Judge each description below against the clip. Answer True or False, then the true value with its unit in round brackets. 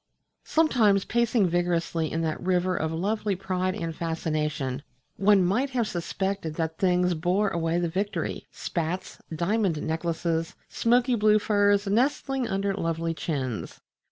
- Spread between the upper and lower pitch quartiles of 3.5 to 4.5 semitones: True (3.9 semitones)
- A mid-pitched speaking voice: True (180 Hz)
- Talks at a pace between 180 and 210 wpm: False (135 wpm)